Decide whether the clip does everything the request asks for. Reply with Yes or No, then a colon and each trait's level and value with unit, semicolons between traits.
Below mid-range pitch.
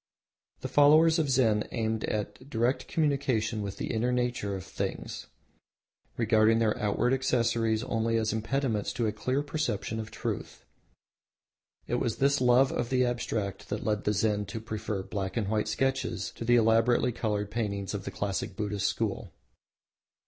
Yes: low, 115 Hz